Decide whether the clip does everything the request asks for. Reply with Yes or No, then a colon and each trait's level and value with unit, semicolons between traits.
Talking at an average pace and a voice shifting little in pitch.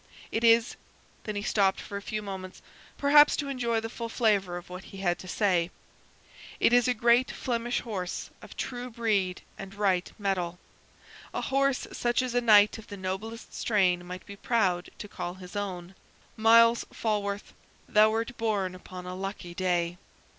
No: average, 175 wpm; average, 3.8 semitones